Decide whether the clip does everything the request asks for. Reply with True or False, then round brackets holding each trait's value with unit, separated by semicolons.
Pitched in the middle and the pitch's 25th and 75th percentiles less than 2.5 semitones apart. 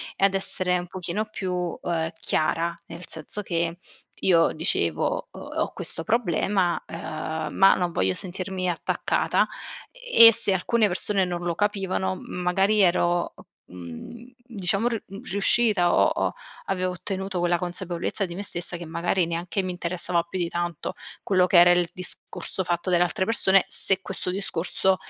True (180 Hz; 2.1 semitones)